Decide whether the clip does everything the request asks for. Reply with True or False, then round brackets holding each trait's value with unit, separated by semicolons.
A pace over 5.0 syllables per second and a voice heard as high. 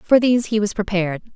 True (7.0 syllables/s; 210 Hz)